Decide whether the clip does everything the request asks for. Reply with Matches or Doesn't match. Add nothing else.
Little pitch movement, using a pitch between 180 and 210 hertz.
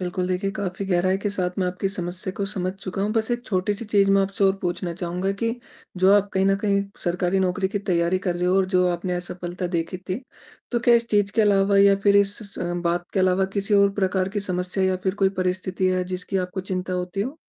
Matches